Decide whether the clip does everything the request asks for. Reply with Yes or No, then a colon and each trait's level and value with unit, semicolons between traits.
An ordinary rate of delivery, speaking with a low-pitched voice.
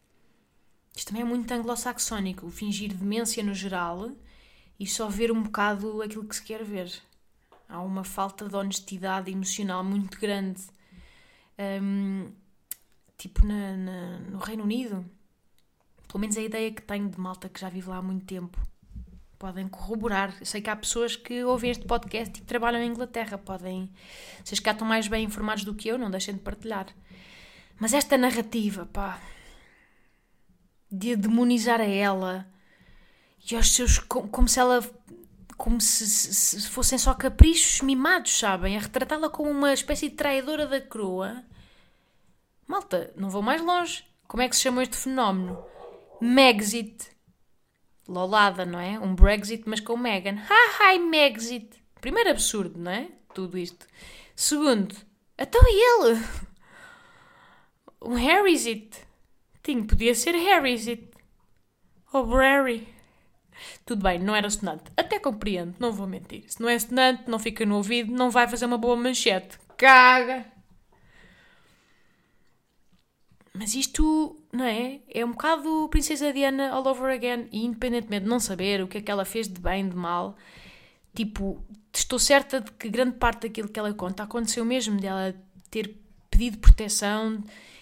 No: average, 150 wpm; high, 225 Hz